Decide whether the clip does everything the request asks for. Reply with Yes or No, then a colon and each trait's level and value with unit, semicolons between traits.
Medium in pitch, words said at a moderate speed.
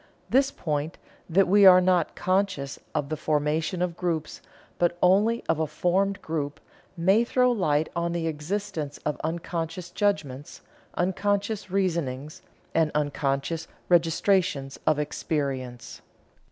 No: medium, 165 Hz; slow, 125 wpm